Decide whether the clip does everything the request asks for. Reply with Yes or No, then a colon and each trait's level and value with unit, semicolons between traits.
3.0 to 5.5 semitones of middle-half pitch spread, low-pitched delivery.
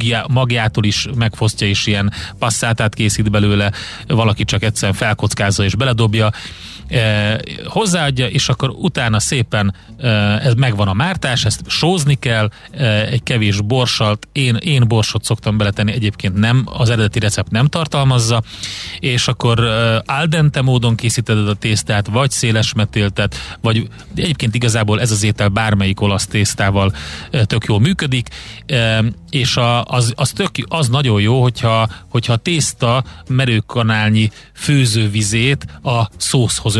Yes: average, 3.3 semitones; low, 115 Hz